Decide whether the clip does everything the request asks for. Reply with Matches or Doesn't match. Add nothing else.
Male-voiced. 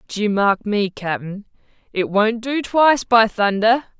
Doesn't match